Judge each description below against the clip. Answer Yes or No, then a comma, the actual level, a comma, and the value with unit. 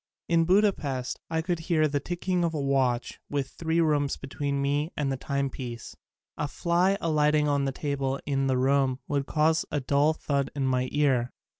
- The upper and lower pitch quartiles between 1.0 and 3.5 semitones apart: Yes, average, 2.9 semitones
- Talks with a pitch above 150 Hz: No, medium, 145 Hz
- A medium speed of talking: Yes, average, 185 wpm